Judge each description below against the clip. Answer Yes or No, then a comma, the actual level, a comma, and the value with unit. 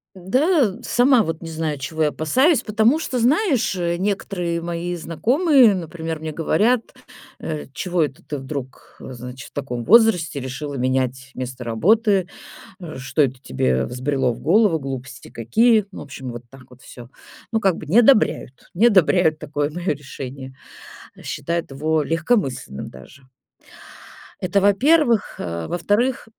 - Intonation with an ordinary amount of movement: No, wide, 7.6 semitones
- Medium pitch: Yes, medium, 165 Hz